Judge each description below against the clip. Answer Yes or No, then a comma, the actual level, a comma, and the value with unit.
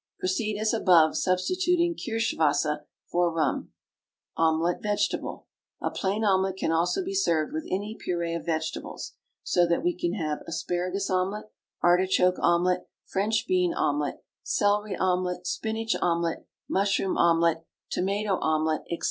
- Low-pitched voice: No, medium, 180 Hz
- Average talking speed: No, slow, 130 wpm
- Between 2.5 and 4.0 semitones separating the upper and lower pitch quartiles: Yes, average, 3.6 semitones